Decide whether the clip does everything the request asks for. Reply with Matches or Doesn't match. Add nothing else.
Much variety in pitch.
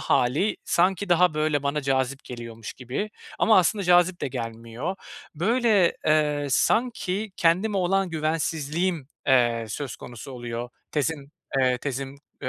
Matches